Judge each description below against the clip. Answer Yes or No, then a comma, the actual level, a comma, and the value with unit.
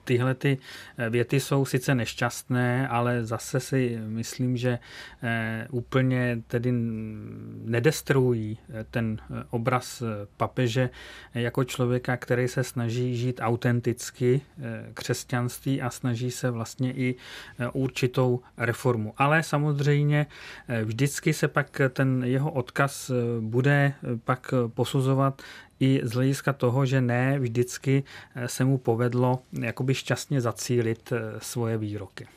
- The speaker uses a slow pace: Yes, slow, 105 wpm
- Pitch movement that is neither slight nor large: No, narrow, 2.0 semitones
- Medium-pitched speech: No, low, 125 Hz